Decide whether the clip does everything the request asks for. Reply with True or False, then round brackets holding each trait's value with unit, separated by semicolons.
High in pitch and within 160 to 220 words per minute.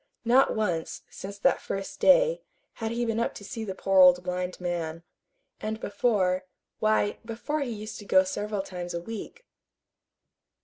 True (205 Hz; 165 wpm)